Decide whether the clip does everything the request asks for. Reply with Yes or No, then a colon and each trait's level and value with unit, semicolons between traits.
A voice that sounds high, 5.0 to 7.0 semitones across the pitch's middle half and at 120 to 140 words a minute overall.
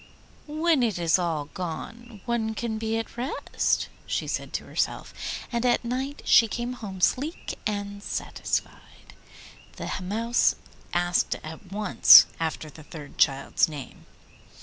Yes: high, 215 Hz; wide, 5.4 semitones; slow, 135 wpm